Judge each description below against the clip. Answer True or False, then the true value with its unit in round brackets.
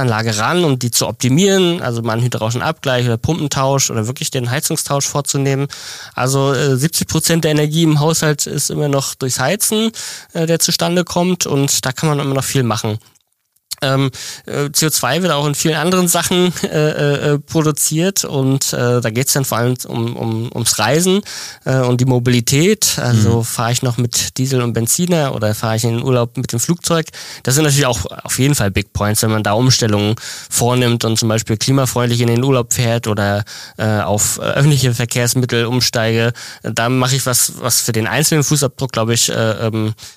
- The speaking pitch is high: False (130 Hz)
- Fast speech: False (175 wpm)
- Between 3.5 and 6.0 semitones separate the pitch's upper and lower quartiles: True (4.4 semitones)